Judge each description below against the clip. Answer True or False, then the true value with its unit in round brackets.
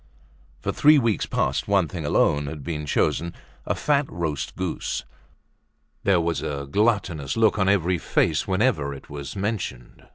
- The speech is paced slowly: False (150 wpm)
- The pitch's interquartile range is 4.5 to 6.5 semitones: True (5.6 semitones)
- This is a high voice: False (85 Hz)